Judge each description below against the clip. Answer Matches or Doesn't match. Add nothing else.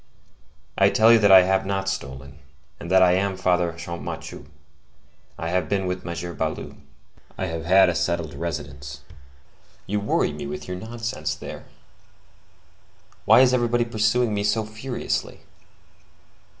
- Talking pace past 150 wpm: Doesn't match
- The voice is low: Matches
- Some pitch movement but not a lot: Matches